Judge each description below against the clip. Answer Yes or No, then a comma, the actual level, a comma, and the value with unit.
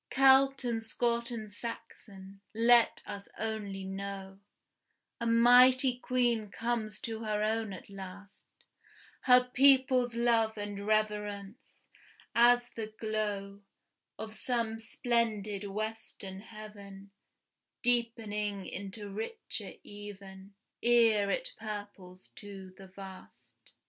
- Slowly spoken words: Yes, slow, 105 wpm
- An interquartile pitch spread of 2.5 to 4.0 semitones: Yes, average, 2.9 semitones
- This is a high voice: Yes, high, 215 Hz